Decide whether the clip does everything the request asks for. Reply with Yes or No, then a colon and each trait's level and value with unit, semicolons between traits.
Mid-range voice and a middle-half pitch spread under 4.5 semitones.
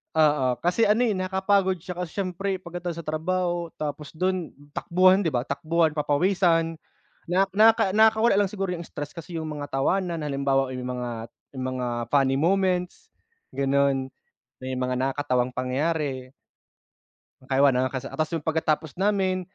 No: medium, 165 Hz; average, 5.2 semitones